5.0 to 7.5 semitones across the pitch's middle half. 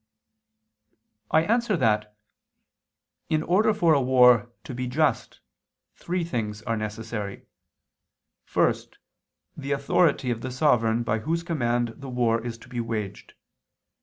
Yes: average, 5.3 semitones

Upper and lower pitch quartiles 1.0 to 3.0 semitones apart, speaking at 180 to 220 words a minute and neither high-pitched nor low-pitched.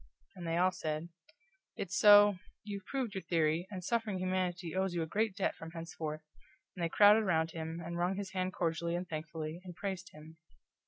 Yes: average, 2.7 semitones; average, 195 wpm; medium, 175 Hz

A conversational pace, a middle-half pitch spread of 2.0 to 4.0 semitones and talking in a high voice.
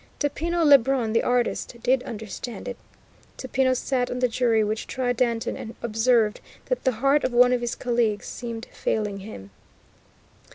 Yes: average, 160 wpm; narrow, 2.5 semitones; high, 245 Hz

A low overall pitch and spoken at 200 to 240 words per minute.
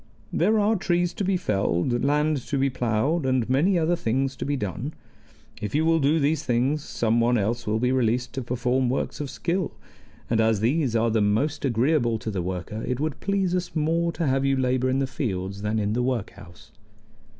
Yes: low, 130 Hz; fast, 205 wpm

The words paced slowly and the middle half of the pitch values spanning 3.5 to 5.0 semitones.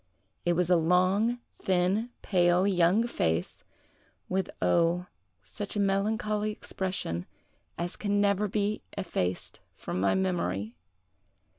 No: slow, 115 wpm; average, 2.9 semitones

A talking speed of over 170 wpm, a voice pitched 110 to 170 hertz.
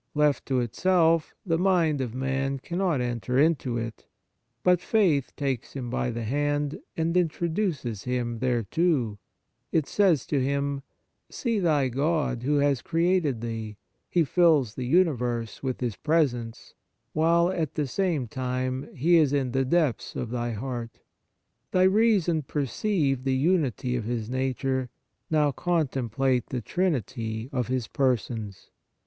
No: average, 145 wpm; low, 135 Hz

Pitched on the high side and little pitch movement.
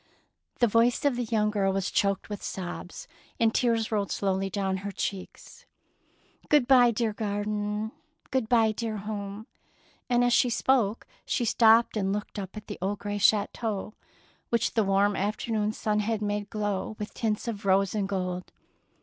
Yes: high, 210 Hz; narrow, 2.3 semitones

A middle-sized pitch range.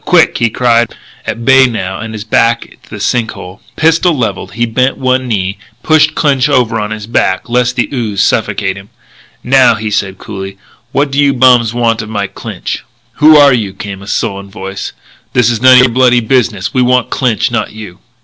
Yes: average, 3.6 semitones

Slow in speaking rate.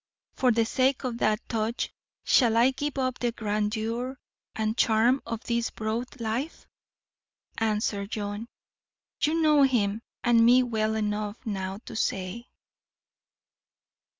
Yes: slow, 125 wpm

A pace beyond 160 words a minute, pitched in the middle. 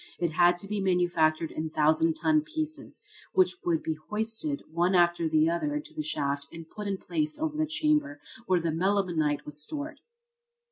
Yes: average, 180 wpm; medium, 180 Hz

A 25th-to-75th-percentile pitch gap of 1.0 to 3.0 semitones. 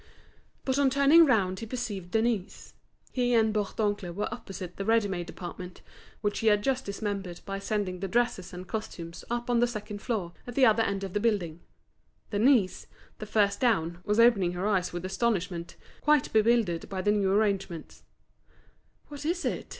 No: average, 4.0 semitones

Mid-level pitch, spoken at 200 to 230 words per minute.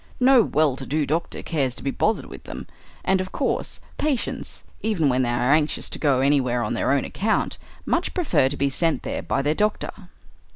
Yes: medium, 150 Hz; fast, 205 wpm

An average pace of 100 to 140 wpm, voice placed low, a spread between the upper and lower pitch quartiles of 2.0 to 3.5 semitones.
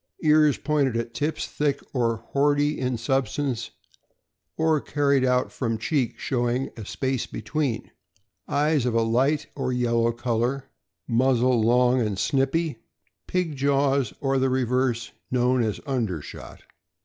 Yes: slow, 135 wpm; low, 130 Hz; average, 3.2 semitones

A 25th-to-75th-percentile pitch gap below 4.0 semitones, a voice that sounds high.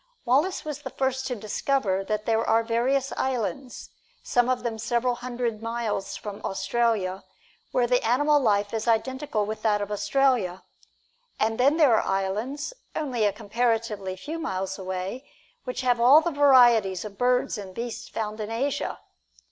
Yes: average, 3.6 semitones; high, 230 Hz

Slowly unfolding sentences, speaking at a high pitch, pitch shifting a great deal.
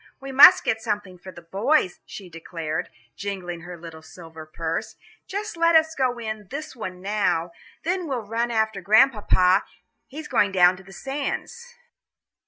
No: average, 160 wpm; high, 205 Hz; wide, 7.1 semitones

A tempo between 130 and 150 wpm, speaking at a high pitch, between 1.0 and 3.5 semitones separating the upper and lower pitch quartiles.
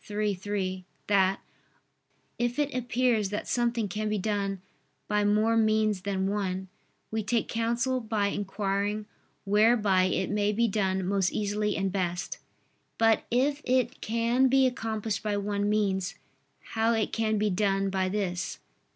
Yes: average, 145 wpm; high, 210 Hz; narrow, 2.5 semitones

